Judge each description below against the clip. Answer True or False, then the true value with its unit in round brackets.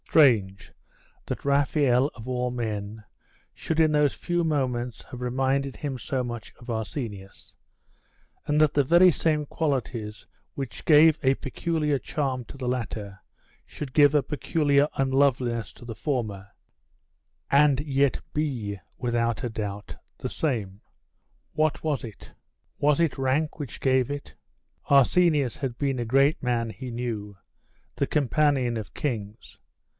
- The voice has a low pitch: True (130 Hz)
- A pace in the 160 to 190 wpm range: False (140 wpm)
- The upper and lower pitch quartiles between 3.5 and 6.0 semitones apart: True (3.8 semitones)